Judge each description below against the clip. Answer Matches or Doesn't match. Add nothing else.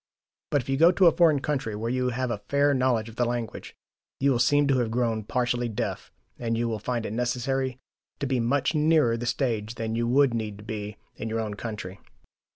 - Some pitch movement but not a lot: Matches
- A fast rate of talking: Matches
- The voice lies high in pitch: Doesn't match